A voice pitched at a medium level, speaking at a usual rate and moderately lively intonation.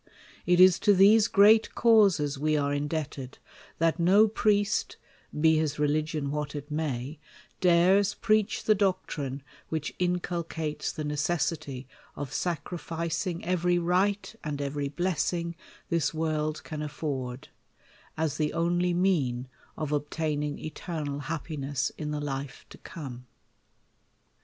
No: medium, 160 Hz; slow, 125 wpm; average, 3.4 semitones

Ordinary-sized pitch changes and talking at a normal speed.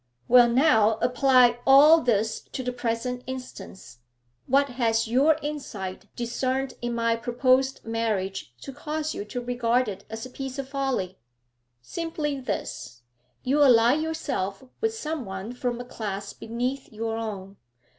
Yes: average, 3.2 semitones; average, 145 wpm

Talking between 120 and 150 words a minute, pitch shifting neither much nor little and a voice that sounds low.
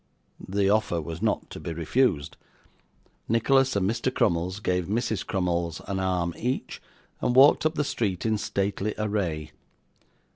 Yes: average, 145 wpm; average, 4.9 semitones; low, 100 Hz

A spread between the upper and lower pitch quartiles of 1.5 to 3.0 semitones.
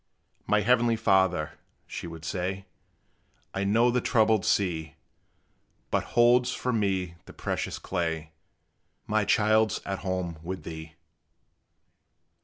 No: average, 4.2 semitones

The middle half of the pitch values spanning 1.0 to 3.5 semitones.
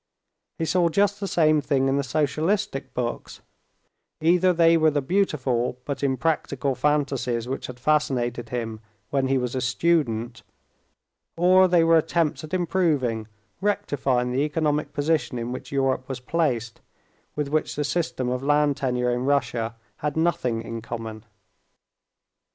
No: average, 4.6 semitones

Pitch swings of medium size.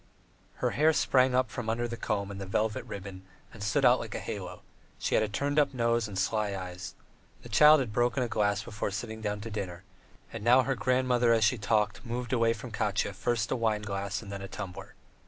Yes: average, 3.1 semitones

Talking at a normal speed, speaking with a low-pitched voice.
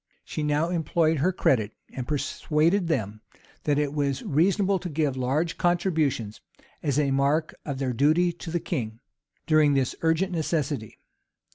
No: average, 150 wpm; medium, 150 Hz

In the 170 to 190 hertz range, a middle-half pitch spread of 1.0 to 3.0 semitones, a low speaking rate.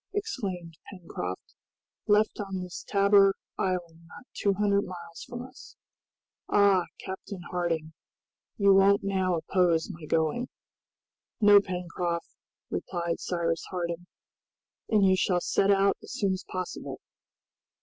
Yes: medium, 185 Hz; narrow, 2.6 semitones; slow, 120 wpm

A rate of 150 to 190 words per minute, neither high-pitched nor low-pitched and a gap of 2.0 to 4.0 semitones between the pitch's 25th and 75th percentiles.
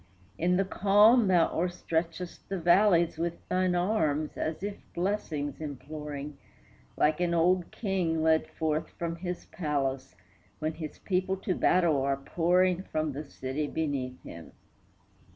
No: slow, 135 wpm; medium, 165 Hz; average, 3.4 semitones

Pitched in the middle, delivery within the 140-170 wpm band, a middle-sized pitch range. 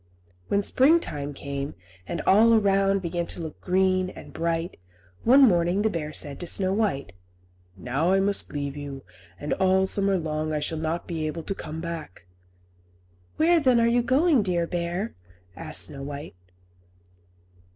Yes: medium, 175 Hz; average, 160 wpm; average, 4.4 semitones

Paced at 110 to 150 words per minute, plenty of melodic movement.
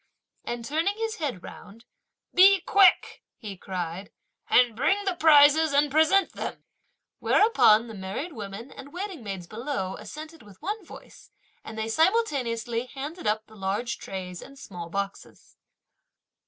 Yes: average, 140 wpm; wide, 7.8 semitones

